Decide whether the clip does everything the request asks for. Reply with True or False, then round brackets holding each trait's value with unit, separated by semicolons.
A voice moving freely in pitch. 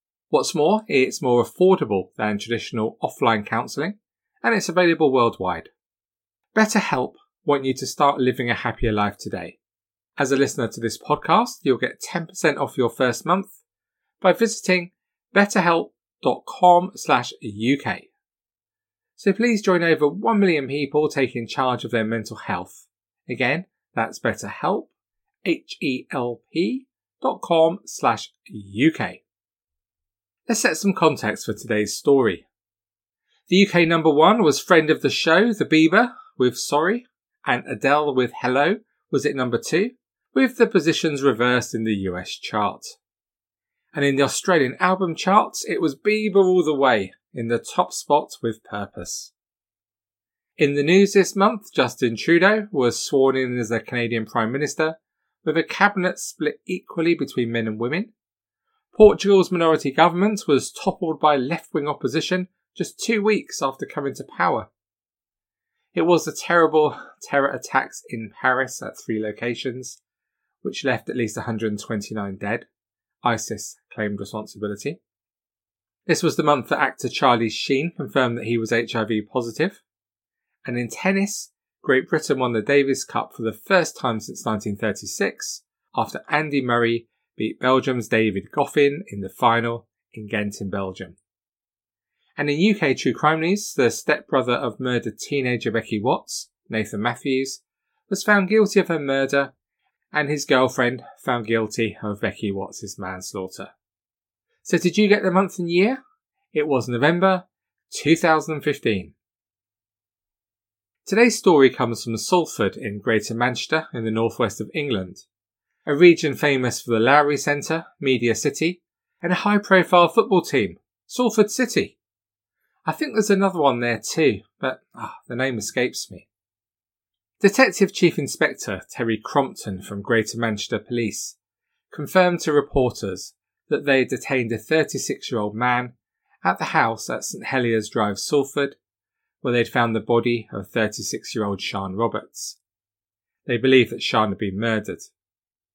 True (7.5 semitones)